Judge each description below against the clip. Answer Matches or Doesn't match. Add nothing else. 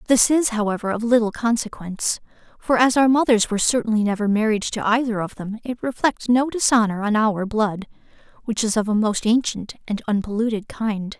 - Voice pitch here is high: Matches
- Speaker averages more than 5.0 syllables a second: Matches